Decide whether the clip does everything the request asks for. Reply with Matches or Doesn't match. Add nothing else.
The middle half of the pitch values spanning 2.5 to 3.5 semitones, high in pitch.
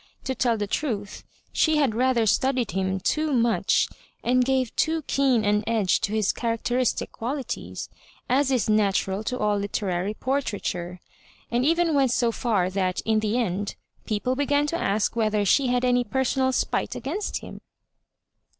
Doesn't match